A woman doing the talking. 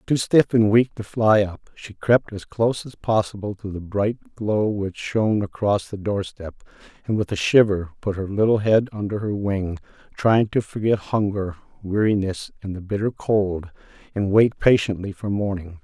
No: male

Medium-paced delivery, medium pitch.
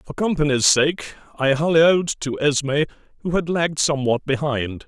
Yes: average, 150 wpm; medium, 145 Hz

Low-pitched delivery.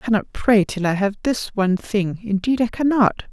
No: high, 210 Hz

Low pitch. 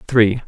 Yes: low, 115 Hz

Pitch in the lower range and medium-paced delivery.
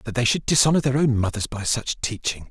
No: low, 125 Hz; fast, 240 wpm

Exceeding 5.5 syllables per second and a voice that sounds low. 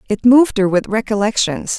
No: 5.7 syllables/s; high, 210 Hz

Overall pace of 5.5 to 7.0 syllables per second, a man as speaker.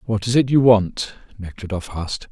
No: 5.1 syllables/s; male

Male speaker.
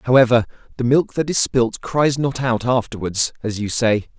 Yes: male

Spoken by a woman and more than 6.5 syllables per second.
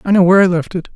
No: male; 8.3 syllables/s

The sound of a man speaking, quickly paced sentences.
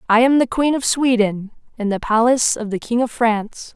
No: female; fast, 225 wpm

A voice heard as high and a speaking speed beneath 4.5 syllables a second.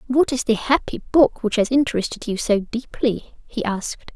No: high, 240 Hz; 5.2 syllables/s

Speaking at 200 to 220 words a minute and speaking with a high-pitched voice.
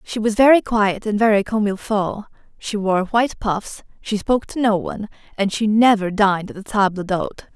Yes: fast, 205 wpm; high, 210 Hz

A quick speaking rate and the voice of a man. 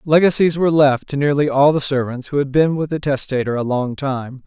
Yes: fast, 230 wpm; male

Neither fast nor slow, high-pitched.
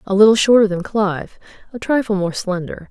Yes: average, 185 wpm; high, 200 Hz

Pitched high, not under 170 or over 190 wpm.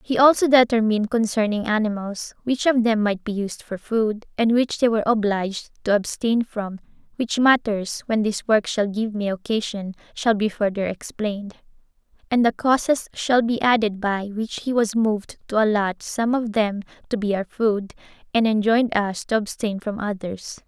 Yes: high, 215 Hz; average, 175 wpm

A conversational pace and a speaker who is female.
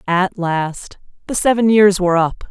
Yes: average, 170 wpm; female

